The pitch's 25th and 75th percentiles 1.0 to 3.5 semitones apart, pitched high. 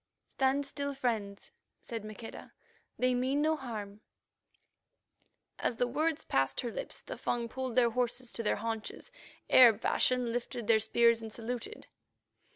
Yes: average, 2.7 semitones; high, 240 Hz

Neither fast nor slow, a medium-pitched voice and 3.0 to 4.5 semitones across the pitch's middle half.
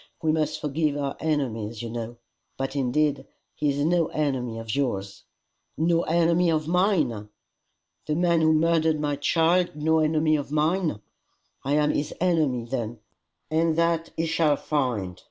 Yes: average, 155 wpm; medium, 150 Hz; average, 3.4 semitones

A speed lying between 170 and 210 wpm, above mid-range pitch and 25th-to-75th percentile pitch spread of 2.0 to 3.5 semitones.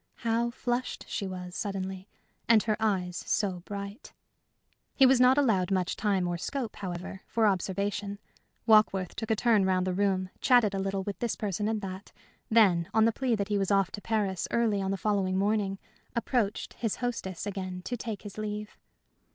Yes: average, 185 wpm; high, 205 Hz; average, 2.7 semitones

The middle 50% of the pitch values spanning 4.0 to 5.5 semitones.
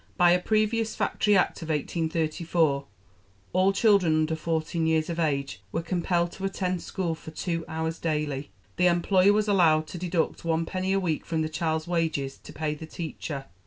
No: narrow, 2.5 semitones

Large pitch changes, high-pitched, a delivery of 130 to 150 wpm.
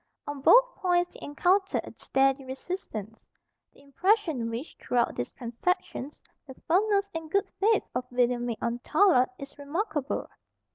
Yes: wide, 7.0 semitones; very high, 285 Hz; average, 145 wpm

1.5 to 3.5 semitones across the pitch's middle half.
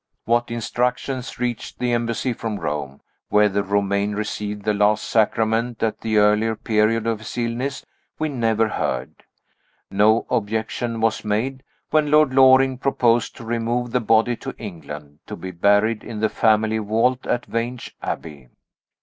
Yes: narrow, 2.5 semitones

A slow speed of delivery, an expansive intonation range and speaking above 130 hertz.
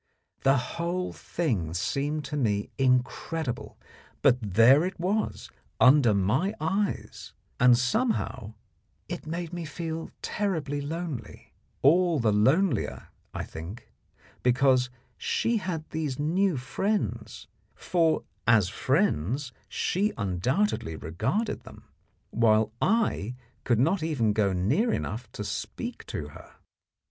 Yes: slow, 115 wpm; wide, 7.3 semitones; medium, 140 Hz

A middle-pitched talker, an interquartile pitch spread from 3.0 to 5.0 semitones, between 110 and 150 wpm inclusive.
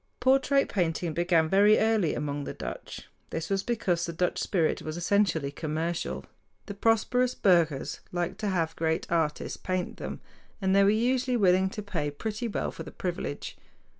No: medium, 180 Hz; average, 4.5 semitones; average, 165 wpm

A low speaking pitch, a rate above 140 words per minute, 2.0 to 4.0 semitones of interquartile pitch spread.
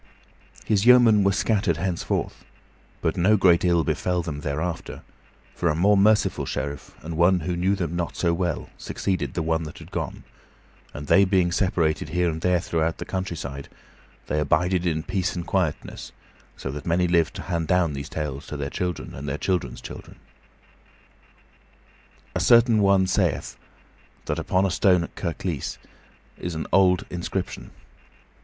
Yes: very low, 85 Hz; average, 160 wpm; average, 2.8 semitones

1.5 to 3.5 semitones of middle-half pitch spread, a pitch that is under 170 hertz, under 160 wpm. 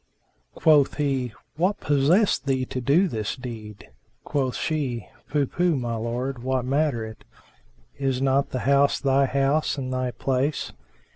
Yes: narrow, 2.4 semitones; low, 135 Hz; average, 145 wpm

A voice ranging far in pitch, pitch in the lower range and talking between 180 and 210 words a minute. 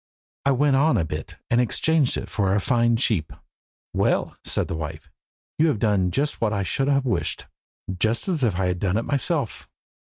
Yes: wide, 6.3 semitones; low, 115 Hz; average, 195 wpm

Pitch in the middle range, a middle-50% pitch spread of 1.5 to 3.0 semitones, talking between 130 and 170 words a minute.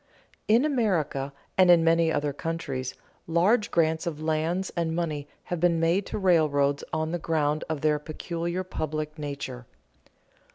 Yes: medium, 160 Hz; narrow, 2.6 semitones; average, 150 wpm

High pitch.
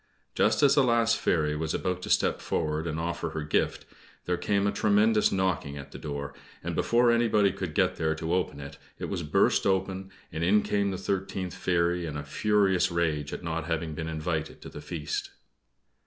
No: very low, 85 Hz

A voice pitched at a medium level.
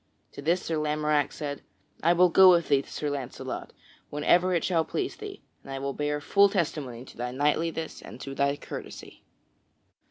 Yes: medium, 150 Hz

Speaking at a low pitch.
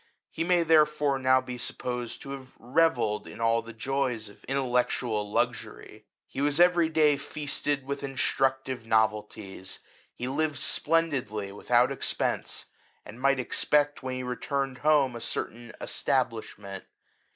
Yes: low, 130 Hz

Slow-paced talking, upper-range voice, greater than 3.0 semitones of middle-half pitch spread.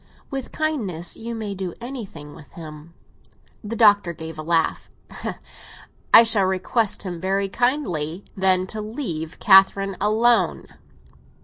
Yes: slow, 125 wpm; high, 195 Hz; average, 4.9 semitones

